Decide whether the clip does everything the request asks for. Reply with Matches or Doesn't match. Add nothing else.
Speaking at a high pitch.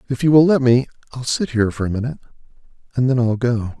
Doesn't match